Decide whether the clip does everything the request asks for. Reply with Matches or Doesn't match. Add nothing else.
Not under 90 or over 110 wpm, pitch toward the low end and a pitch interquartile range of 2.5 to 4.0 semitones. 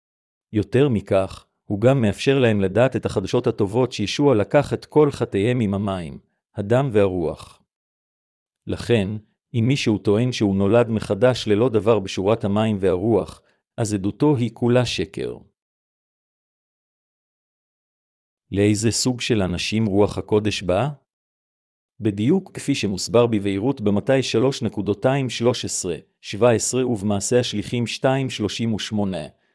Matches